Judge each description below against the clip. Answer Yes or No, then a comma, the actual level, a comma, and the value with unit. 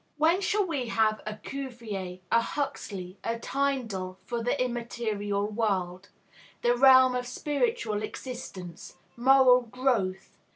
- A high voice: Yes, high, 235 Hz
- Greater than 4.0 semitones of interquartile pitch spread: Yes, average, 4.4 semitones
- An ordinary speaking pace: No, slow, 120 wpm